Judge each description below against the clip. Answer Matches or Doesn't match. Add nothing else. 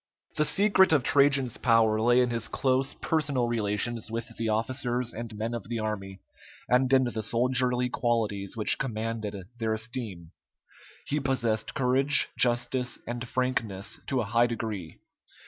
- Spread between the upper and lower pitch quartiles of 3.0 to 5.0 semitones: Doesn't match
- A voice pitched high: Doesn't match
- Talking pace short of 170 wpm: Matches